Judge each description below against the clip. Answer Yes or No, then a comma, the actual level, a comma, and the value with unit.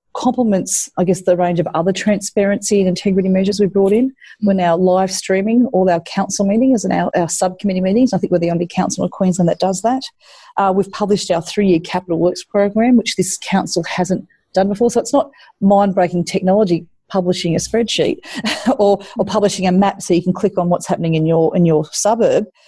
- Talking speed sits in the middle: No, fast, 210 wpm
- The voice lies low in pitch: No, high, 195 Hz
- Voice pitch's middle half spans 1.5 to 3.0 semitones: Yes, narrow, 2.6 semitones